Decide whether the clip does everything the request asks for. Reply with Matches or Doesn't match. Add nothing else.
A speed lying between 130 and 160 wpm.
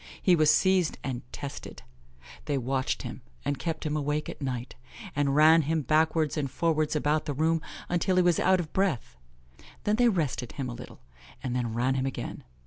Doesn't match